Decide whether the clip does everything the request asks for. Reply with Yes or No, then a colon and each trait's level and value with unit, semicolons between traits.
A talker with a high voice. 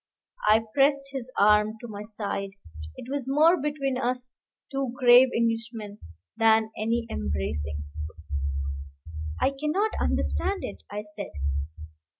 Yes: high, 235 Hz